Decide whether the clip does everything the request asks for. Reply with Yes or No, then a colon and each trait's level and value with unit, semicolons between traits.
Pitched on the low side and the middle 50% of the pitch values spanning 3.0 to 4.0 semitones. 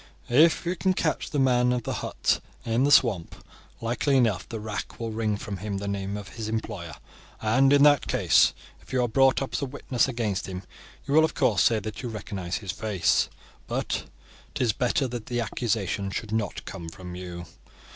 No: low, 115 Hz; average, 4.4 semitones